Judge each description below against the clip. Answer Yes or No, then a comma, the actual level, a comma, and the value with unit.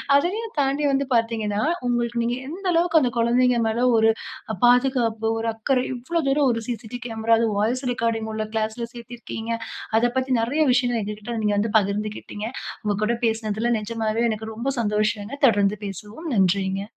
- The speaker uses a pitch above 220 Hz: Yes, high, 230 Hz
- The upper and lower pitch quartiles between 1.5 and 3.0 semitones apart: Yes, narrow, 2.5 semitones